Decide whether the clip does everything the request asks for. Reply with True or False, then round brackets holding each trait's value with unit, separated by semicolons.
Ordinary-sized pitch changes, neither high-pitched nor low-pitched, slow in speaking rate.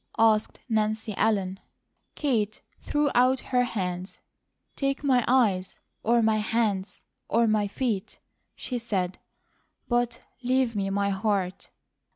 False (3.5 semitones; 220 Hz; 120 wpm)